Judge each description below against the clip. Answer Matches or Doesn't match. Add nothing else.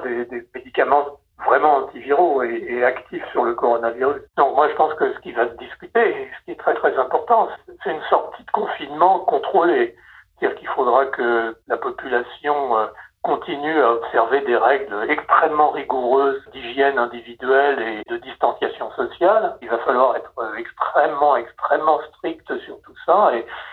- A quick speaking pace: Doesn't match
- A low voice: Doesn't match